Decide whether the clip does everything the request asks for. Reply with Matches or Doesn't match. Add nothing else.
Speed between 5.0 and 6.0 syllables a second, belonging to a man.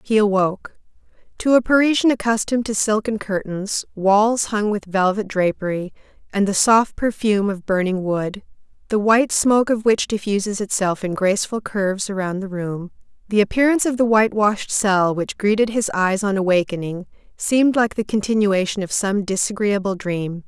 Doesn't match